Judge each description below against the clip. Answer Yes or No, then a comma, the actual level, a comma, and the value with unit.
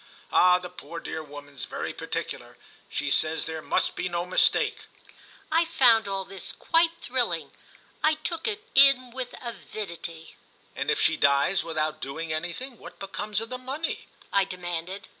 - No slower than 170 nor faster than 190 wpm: No, average, 150 wpm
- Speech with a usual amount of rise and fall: No, wide, 8.0 semitones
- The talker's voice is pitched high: Yes, high, 195 Hz